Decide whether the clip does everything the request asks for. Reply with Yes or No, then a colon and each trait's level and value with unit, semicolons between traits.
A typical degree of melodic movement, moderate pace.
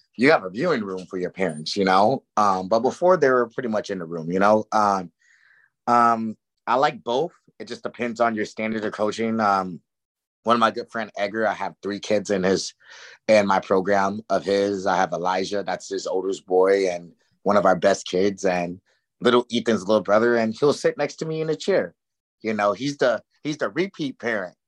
No: average, 3.7 semitones; fast, 215 wpm